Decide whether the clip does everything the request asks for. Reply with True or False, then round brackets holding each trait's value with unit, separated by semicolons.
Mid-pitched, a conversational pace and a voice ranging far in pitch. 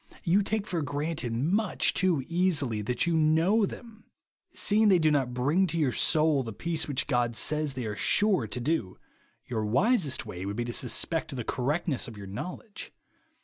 True (150 Hz; 185 wpm; 6.4 semitones)